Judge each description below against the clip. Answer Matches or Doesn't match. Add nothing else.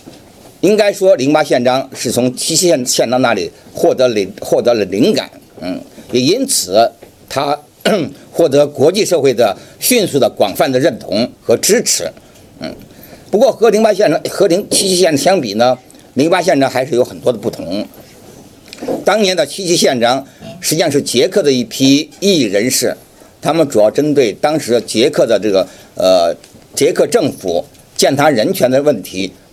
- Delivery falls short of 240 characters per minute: Doesn't match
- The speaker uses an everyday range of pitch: Doesn't match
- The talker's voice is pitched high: Doesn't match